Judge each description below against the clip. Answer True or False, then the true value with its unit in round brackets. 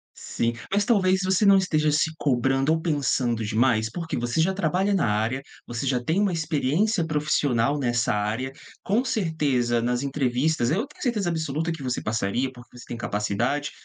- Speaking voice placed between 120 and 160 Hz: True (140 Hz)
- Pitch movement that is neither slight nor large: False (5.9 semitones)